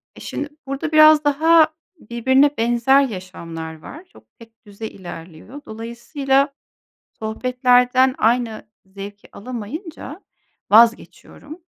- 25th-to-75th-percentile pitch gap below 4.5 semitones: No, average, 4.8 semitones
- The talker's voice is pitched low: No, high, 245 Hz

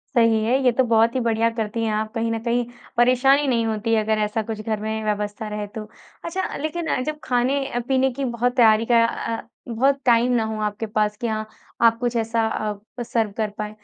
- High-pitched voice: Yes, high, 230 Hz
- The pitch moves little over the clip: Yes, narrow, 2.1 semitones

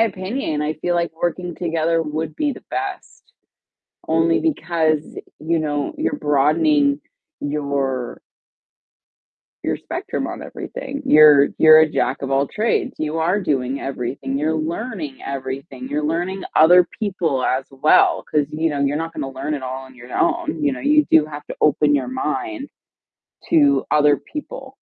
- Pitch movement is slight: No, average, 4.0 semitones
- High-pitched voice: No, medium, 155 Hz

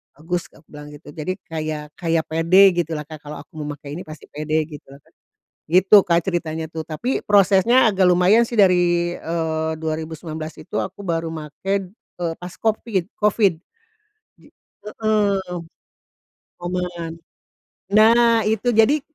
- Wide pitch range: No, average, 4.1 semitones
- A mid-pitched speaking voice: Yes, medium, 175 Hz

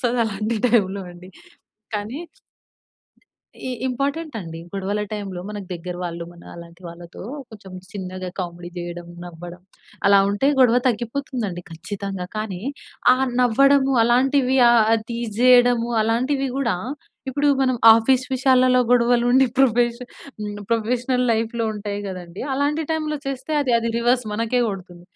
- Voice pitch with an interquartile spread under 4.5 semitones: No, average, 4.9 semitones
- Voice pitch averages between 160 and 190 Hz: No, high, 230 Hz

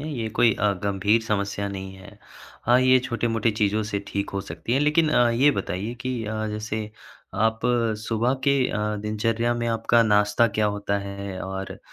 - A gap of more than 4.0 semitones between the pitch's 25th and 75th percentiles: No, average, 2.7 semitones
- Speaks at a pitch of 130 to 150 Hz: No, low, 110 Hz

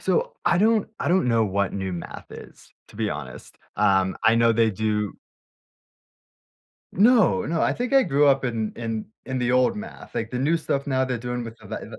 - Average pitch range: No, wide, 6.7 semitones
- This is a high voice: No, low, 125 Hz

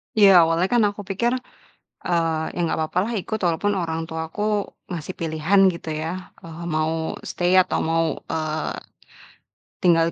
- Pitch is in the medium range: Yes, medium, 170 Hz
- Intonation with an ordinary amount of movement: Yes, average, 3.1 semitones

